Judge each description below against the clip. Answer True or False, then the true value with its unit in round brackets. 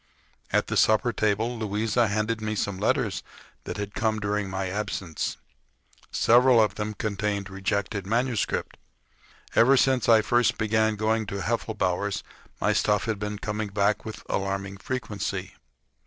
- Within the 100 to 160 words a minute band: True (140 wpm)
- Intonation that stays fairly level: True (1.9 semitones)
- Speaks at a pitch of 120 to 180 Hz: False (105 Hz)